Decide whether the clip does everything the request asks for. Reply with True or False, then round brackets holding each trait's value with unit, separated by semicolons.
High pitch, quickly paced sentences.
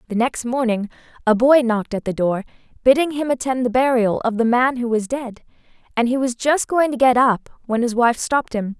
True (245 Hz; 225 wpm)